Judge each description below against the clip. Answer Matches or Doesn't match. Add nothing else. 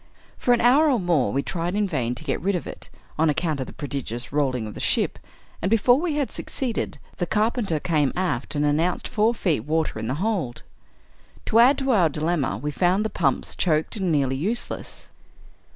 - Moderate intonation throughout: Doesn't match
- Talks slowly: Doesn't match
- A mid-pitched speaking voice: Matches